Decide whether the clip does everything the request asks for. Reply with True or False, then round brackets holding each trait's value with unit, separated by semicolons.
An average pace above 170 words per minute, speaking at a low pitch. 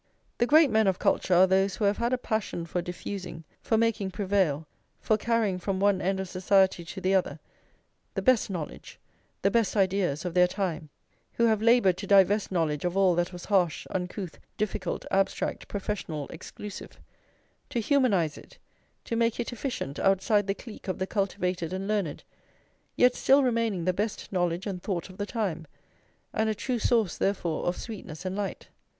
False (180 wpm; 195 Hz)